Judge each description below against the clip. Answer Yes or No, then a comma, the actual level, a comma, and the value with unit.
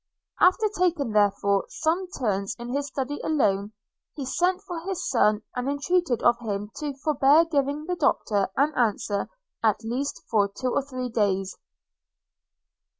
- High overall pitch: Yes, very high, 260 Hz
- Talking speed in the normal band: Yes, average, 150 wpm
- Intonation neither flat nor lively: No, wide, 6.4 semitones